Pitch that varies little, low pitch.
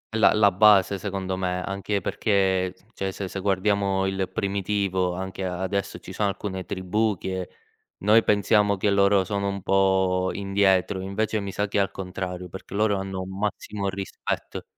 Yes: narrow, 1.2 semitones; very low, 95 Hz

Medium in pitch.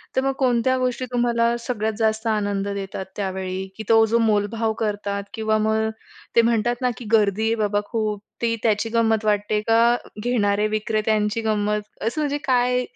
No: high, 220 Hz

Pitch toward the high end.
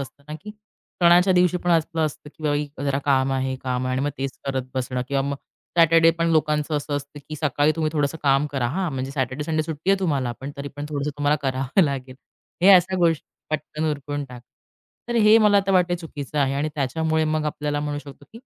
No: medium, 150 Hz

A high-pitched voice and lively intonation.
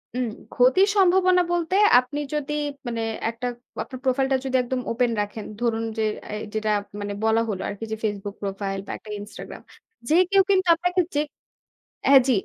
Yes: very high, 250 Hz; wide, 5.9 semitones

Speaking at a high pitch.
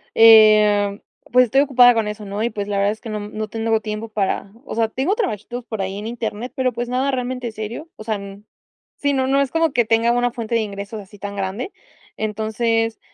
Yes: high, 225 Hz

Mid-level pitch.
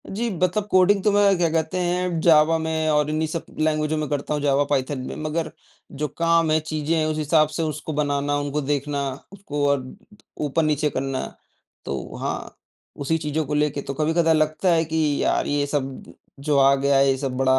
Yes: medium, 155 Hz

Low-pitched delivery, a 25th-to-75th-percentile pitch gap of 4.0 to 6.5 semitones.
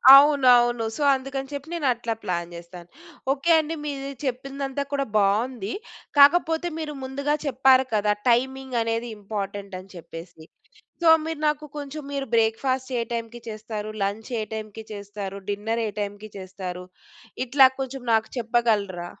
No: high, 235 Hz; average, 5.0 semitones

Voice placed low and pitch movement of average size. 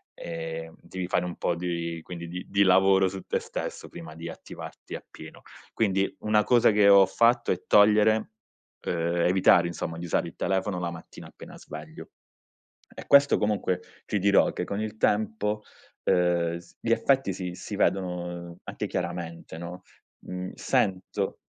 Yes: very low, 90 Hz; average, 3.2 semitones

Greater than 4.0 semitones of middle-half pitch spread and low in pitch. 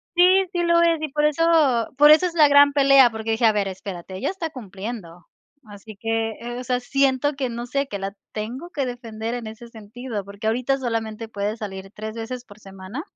No: average, 4.5 semitones; high, 235 Hz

